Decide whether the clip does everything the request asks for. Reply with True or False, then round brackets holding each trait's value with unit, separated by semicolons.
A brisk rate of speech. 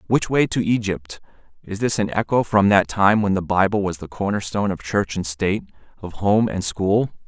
True (215 wpm)